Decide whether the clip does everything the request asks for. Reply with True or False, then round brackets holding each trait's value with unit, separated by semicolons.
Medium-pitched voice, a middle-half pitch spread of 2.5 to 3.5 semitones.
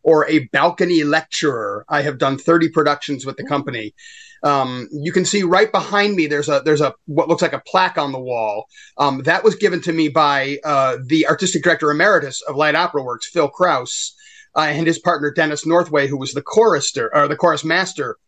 False (160 Hz; 4.3 semitones)